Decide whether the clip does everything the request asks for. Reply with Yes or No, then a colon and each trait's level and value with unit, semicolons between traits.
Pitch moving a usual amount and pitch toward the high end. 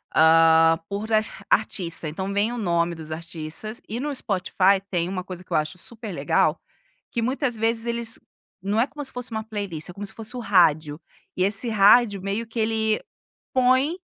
Yes: average, 4.7 semitones; high, 205 Hz